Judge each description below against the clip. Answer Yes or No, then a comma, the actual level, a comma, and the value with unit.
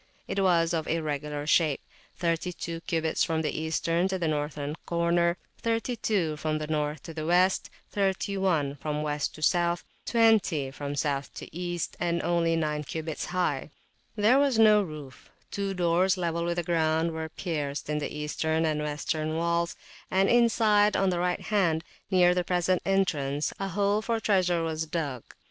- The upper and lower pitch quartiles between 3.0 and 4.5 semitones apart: Yes, average, 3.3 semitones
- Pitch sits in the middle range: Yes, medium, 170 Hz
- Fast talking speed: No, average, 160 wpm